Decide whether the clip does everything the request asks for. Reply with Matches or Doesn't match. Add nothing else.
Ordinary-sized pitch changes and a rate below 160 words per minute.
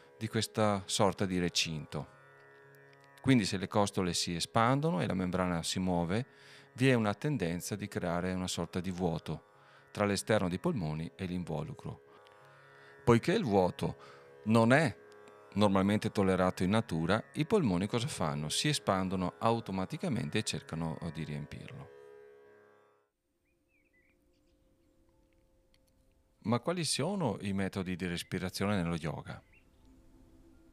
Matches